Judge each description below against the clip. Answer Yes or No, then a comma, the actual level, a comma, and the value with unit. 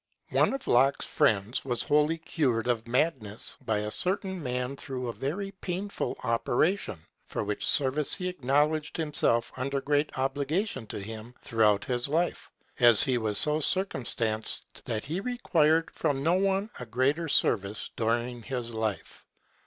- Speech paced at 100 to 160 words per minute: Yes, average, 155 wpm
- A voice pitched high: No, low, 135 Hz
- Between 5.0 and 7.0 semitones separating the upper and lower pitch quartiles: Yes, wide, 5.5 semitones